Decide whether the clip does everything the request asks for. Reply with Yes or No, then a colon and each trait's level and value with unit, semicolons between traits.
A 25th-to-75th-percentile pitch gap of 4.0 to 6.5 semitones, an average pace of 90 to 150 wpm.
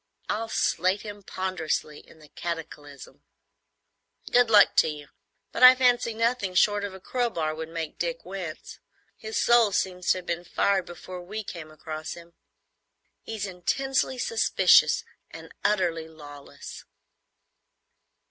Yes: average, 5.1 semitones; slow, 135 wpm